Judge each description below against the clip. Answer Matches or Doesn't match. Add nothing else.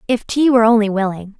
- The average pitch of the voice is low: Doesn't match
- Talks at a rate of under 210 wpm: Doesn't match